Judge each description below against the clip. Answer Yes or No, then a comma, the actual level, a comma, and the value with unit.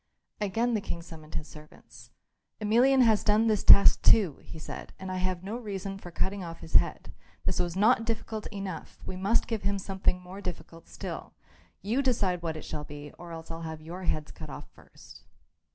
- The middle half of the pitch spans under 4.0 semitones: No, average, 4.3 semitones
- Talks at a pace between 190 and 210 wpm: Yes, average, 200 wpm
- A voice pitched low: No, high, 190 Hz